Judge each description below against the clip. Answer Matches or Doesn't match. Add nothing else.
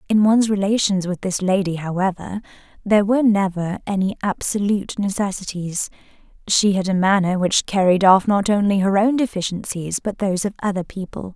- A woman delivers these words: Matches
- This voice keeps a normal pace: Matches